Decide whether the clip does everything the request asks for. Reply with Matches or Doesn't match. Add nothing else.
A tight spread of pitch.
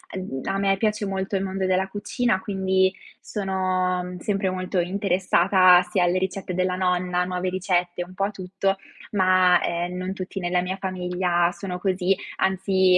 Matches